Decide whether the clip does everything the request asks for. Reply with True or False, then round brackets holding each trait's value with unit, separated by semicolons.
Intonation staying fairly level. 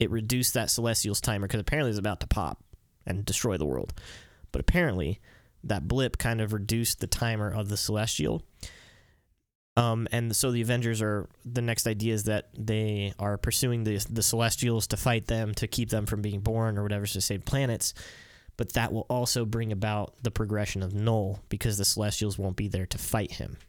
True (2.1 semitones)